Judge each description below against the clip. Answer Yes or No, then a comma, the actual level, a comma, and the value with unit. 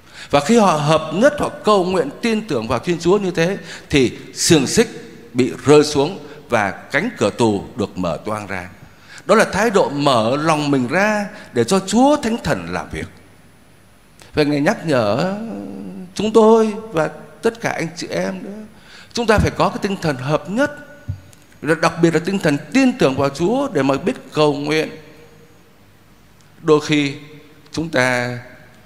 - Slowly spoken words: No, average, 175 wpm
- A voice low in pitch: No, medium, 160 Hz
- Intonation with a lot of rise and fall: Yes, wide, 6.7 semitones